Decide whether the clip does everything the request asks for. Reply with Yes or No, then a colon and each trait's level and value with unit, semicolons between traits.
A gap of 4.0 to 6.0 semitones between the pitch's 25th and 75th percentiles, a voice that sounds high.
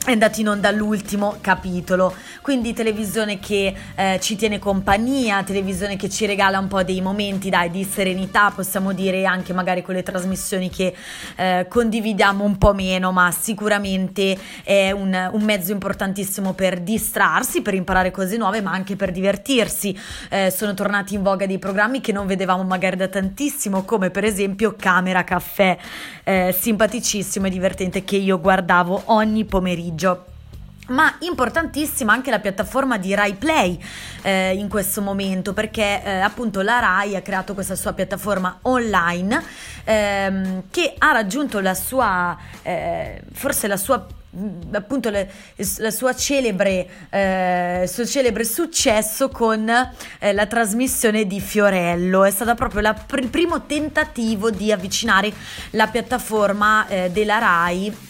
No: narrow, 2.6 semitones; high, 200 Hz